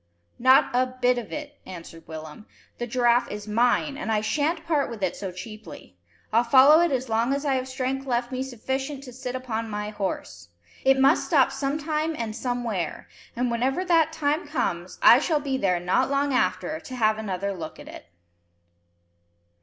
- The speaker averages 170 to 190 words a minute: Yes, average, 185 wpm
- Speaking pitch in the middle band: No, very high, 250 Hz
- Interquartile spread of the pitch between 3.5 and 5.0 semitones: Yes, average, 4.3 semitones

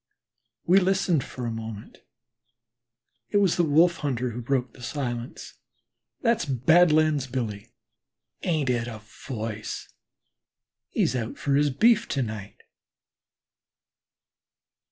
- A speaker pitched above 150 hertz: No, low, 130 Hz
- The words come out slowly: Yes, slow, 110 wpm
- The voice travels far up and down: Yes, wide, 5.7 semitones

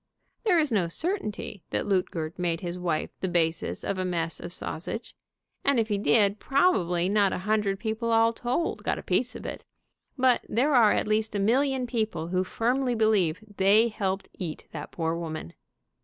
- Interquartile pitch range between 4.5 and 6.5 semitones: Yes, average, 4.8 semitones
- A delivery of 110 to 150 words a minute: No, average, 185 wpm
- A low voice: No, high, 205 Hz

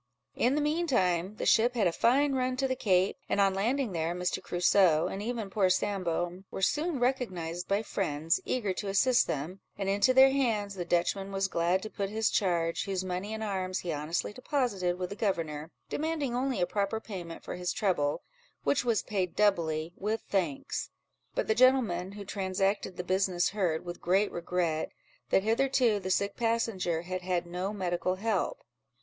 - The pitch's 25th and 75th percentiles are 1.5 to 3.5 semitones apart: No, average, 4.1 semitones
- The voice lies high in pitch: Yes, high, 195 Hz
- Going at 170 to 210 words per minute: Yes, average, 185 wpm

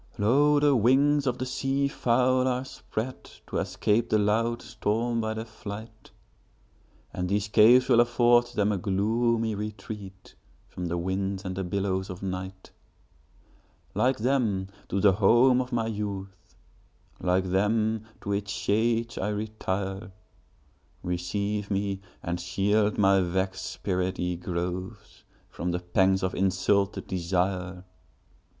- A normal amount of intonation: Yes, average, 3.7 semitones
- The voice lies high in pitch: No, low, 100 Hz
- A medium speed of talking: No, slow, 120 wpm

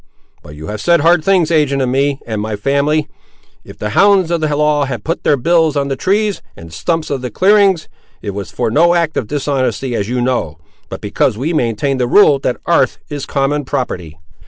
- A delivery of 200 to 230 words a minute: Yes, fast, 205 wpm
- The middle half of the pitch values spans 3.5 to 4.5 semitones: No, average, 5.0 semitones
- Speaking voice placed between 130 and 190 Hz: Yes, medium, 140 Hz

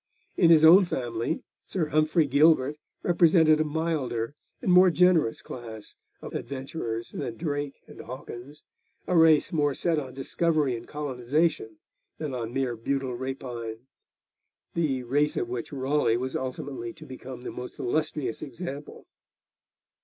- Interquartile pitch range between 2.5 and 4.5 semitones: Yes, average, 4.1 semitones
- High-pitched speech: No, medium, 140 Hz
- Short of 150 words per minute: Yes, average, 140 wpm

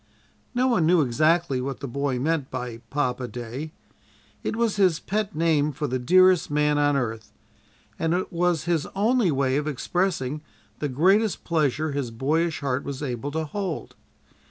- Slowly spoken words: No, average, 165 wpm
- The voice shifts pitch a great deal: No, average, 4.6 semitones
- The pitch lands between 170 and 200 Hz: No, medium, 150 Hz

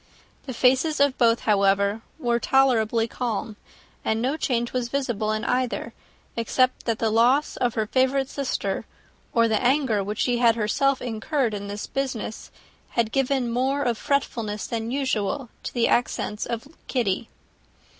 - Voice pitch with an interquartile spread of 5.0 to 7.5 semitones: No, average, 3.1 semitones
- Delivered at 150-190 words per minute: Yes, average, 155 wpm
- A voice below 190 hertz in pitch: No, high, 235 Hz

